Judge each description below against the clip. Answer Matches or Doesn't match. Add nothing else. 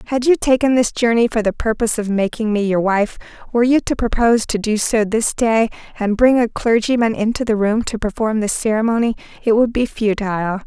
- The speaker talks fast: Matches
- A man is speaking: Doesn't match